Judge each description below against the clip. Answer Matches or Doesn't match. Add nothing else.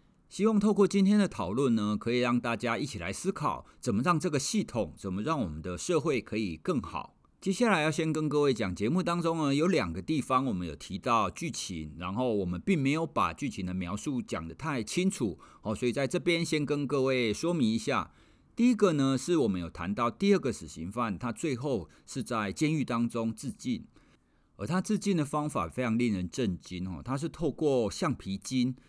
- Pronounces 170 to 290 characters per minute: Doesn't match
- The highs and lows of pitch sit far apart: Matches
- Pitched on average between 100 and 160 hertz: Matches